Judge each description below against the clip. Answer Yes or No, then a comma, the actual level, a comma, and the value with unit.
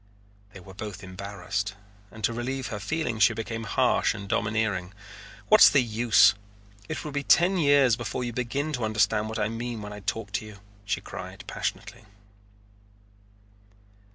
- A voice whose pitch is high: No, low, 110 Hz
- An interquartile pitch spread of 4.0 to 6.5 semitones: No, average, 3.2 semitones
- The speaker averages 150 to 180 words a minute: Yes, average, 160 wpm